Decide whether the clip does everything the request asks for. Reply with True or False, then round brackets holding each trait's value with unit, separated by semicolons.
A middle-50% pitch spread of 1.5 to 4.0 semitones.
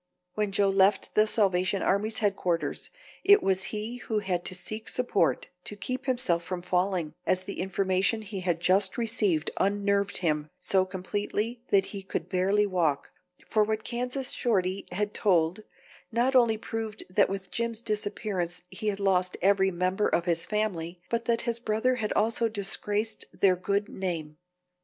True (3.0 semitones)